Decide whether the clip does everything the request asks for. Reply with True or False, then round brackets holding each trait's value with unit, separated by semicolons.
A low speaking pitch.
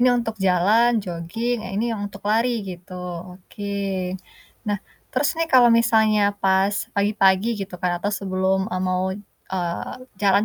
False (200 Hz)